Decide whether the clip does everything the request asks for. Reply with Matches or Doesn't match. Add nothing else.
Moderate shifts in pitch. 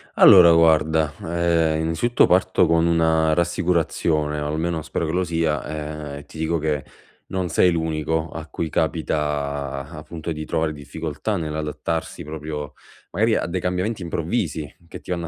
Doesn't match